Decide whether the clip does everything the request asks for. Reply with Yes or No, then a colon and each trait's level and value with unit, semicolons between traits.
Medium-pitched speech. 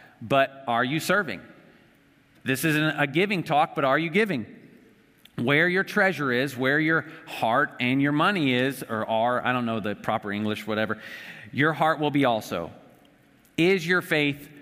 Yes: medium, 145 Hz